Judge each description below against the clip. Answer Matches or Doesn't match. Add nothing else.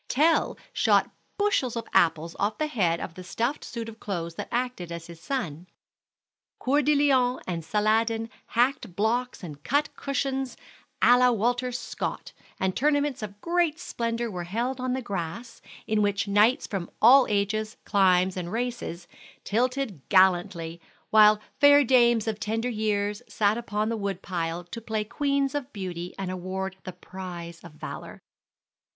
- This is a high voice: Matches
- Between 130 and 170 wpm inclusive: Matches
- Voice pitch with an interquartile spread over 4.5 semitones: Matches